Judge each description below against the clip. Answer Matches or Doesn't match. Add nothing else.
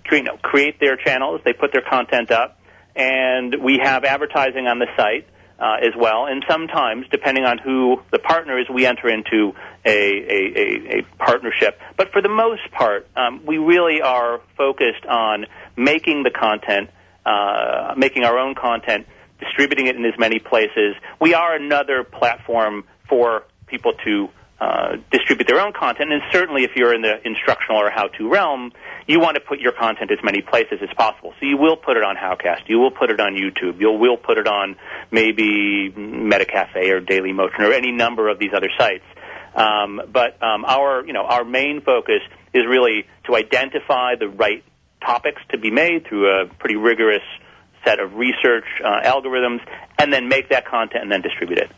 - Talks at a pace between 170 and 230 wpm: Matches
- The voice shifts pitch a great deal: Matches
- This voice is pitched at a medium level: Doesn't match